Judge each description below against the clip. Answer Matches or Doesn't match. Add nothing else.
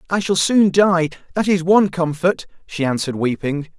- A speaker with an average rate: Matches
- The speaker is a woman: Doesn't match